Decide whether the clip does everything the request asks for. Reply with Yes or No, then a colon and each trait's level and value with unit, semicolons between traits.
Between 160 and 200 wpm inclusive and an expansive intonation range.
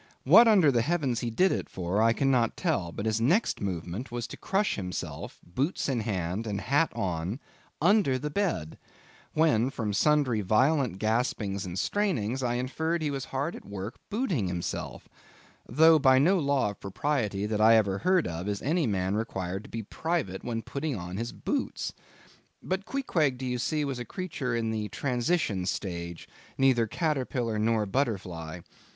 Yes: average, 165 wpm; wide, 6.8 semitones